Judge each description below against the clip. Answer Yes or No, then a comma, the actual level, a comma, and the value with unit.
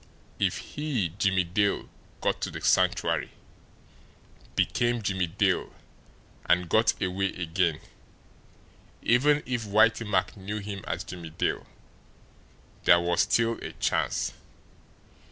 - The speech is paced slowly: Yes, slow, 115 wpm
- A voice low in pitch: Yes, low, 100 Hz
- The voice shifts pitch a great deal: No, average, 4.1 semitones